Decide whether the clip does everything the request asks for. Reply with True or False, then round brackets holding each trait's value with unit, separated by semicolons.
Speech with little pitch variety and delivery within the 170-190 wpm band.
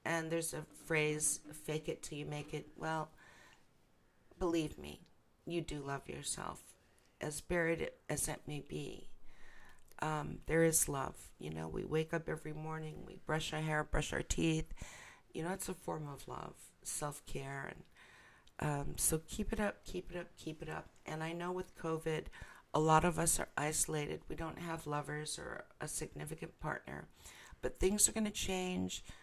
True (1.9 semitones; 175 wpm)